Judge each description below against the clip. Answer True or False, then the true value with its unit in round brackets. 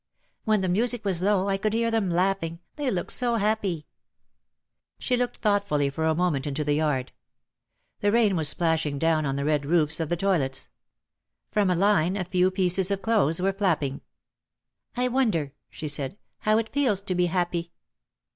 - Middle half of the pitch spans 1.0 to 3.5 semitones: False (4.7 semitones)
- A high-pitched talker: False (180 Hz)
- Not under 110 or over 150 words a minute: False (190 wpm)